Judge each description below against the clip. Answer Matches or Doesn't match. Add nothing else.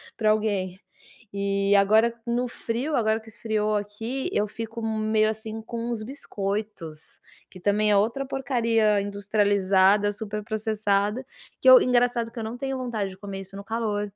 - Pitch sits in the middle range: Doesn't match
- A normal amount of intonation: Doesn't match